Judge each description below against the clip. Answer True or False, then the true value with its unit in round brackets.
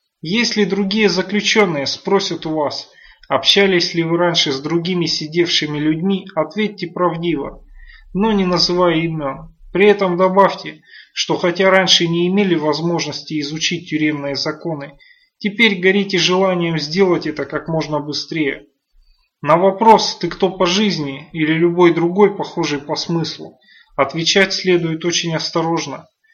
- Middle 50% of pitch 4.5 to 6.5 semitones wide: False (3.5 semitones)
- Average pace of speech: True (130 wpm)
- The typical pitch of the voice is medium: True (175 Hz)